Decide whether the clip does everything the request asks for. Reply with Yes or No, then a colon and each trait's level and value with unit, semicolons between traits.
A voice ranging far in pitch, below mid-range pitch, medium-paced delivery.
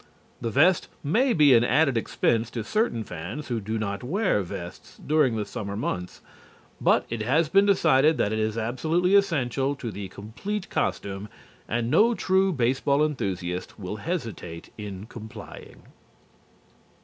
Yes: wide, 6.8 semitones; low, 120 Hz; average, 150 wpm